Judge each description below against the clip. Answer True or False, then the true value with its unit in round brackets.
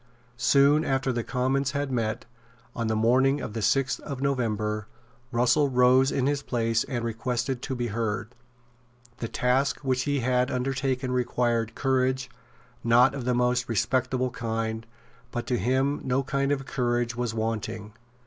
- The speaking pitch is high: False (125 Hz)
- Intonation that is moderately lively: False (2.3 semitones)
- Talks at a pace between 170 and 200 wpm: False (155 wpm)